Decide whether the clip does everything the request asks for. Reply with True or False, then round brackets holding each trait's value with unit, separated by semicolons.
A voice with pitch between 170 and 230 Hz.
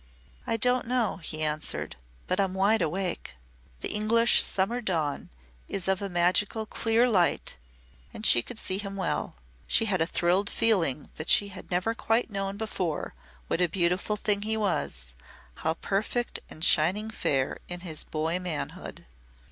True (190 Hz)